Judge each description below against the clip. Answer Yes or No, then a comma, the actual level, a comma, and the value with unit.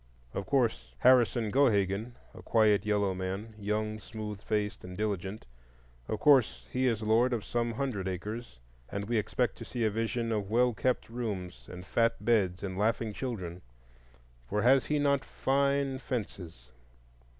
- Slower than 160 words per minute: Yes, average, 150 wpm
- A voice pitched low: Yes, low, 110 Hz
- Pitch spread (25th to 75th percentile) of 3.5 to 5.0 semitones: Yes, average, 3.8 semitones